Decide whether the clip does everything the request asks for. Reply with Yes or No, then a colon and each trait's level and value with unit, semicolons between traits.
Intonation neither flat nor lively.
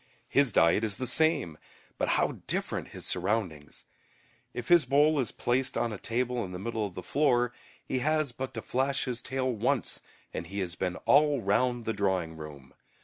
No: wide, 5.8 semitones